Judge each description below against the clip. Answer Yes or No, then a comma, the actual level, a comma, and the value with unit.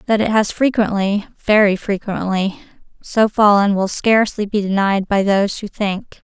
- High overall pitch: Yes, high, 205 Hz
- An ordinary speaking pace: Yes, average, 150 wpm